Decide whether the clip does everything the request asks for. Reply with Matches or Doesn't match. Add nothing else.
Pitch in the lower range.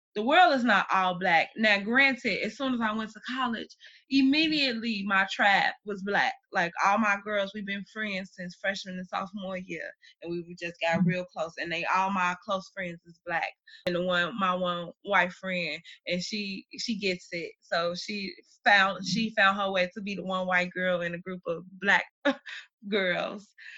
Doesn't match